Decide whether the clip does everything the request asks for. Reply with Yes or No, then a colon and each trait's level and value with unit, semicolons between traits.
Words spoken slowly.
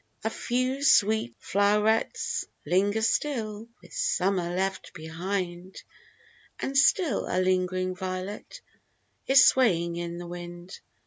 Yes: slow, 115 wpm